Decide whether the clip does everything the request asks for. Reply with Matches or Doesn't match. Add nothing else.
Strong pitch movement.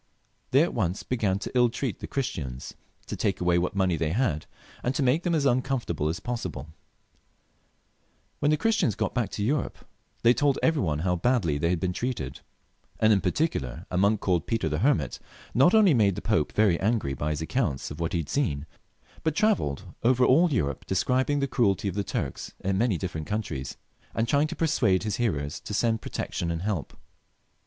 Matches